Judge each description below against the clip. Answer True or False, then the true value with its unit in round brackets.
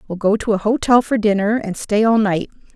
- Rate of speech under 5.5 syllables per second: False (5.6 syllables/s)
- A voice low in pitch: False (215 Hz)